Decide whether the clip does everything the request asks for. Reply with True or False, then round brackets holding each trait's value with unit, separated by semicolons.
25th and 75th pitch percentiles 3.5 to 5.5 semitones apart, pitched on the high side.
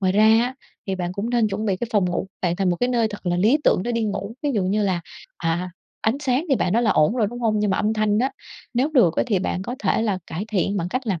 True (3.9 semitones; 210 Hz)